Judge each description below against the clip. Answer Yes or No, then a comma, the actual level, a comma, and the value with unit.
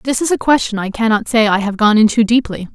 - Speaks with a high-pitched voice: Yes, high, 225 Hz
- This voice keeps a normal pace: No, fast, 260 wpm